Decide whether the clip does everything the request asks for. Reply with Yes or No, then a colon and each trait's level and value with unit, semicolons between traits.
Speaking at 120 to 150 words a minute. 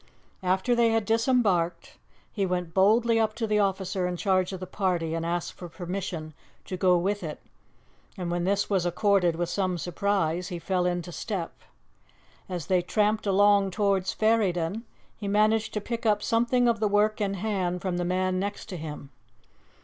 No: average, 180 wpm